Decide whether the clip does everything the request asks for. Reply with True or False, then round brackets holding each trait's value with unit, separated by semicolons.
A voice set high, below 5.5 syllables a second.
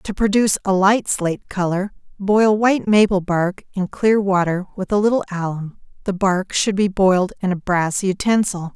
True (195 Hz; 4.9 syllables/s)